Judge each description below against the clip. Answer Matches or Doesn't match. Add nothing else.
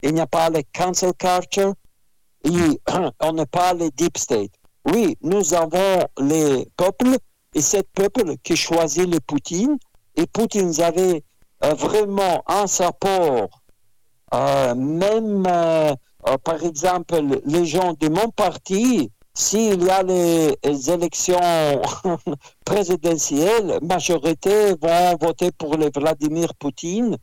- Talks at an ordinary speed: Doesn't match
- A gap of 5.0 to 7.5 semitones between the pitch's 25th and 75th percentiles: Doesn't match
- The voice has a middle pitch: Matches